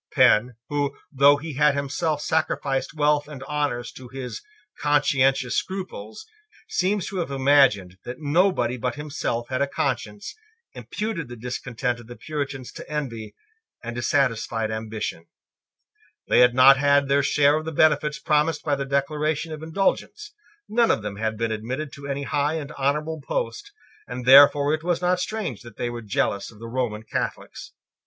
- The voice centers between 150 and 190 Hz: No, medium, 140 Hz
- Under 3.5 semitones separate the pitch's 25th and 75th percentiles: No, average, 3.8 semitones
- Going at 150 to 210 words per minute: Yes, average, 165 wpm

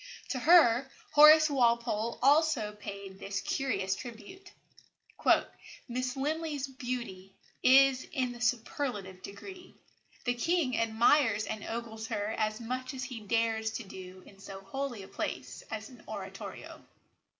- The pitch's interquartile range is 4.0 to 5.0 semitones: Yes, average, 4.3 semitones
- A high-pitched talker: Yes, high, 235 Hz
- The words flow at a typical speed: No, slow, 130 wpm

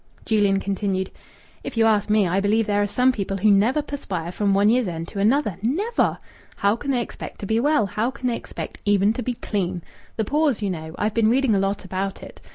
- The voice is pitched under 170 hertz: No, high, 210 Hz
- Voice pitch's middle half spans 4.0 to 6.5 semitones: No, average, 3.3 semitones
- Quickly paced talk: Yes, fast, 230 wpm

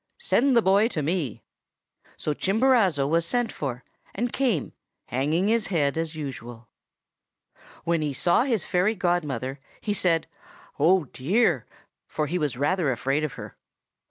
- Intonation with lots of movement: Yes, wide, 6.0 semitones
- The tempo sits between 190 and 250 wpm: No, average, 145 wpm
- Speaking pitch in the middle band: Yes, medium, 165 Hz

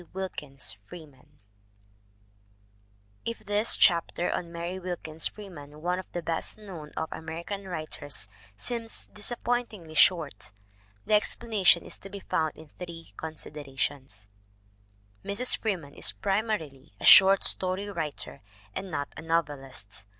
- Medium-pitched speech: Yes, medium, 170 Hz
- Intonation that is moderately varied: Yes, average, 4.8 semitones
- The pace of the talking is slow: Yes, slow, 125 wpm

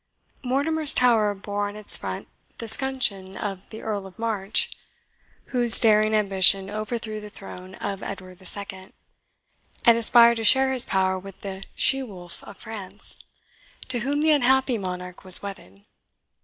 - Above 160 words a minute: No, average, 150 wpm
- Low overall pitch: No, high, 210 Hz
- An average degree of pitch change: Yes, average, 3.7 semitones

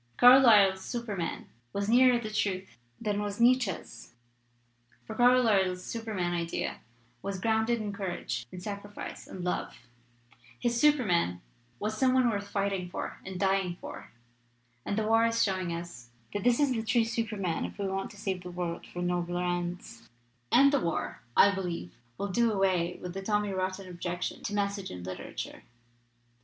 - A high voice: Yes, high, 195 Hz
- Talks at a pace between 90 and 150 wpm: No, average, 165 wpm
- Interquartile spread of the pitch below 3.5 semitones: No, average, 3.9 semitones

